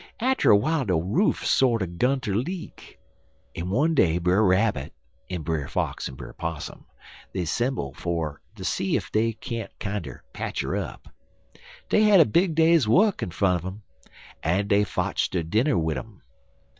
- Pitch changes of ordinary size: No, wide, 7.2 semitones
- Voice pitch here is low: Yes, low, 100 Hz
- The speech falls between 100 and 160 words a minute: No, average, 170 wpm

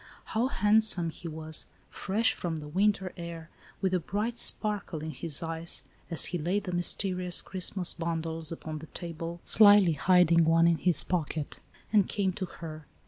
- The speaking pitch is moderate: Yes, medium, 170 Hz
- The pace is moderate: Yes, average, 165 wpm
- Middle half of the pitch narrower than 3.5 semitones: Yes, average, 2.9 semitones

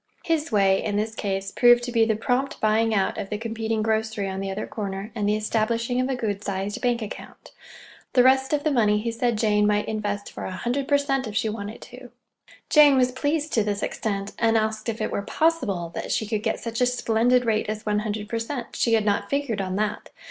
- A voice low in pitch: No, high, 220 Hz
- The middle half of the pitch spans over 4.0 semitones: No, average, 2.9 semitones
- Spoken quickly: Yes, fast, 230 wpm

